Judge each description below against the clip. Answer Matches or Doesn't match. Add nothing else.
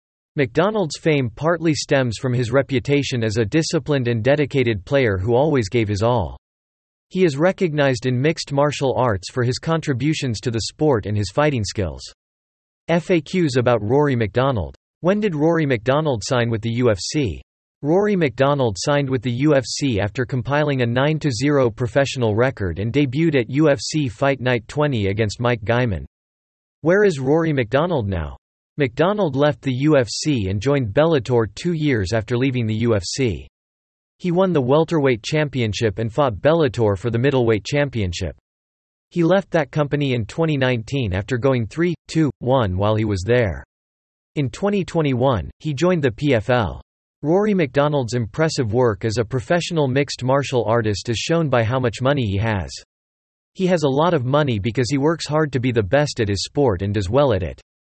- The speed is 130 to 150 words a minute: Doesn't match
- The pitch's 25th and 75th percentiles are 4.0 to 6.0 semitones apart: Matches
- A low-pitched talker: Matches